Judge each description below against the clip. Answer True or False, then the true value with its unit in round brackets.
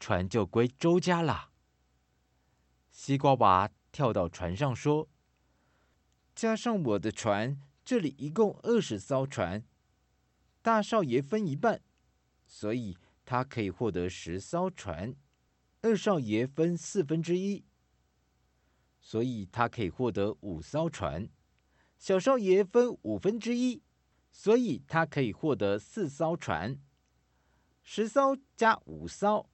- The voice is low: True (115 Hz)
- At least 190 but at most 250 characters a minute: False (170 characters per minute)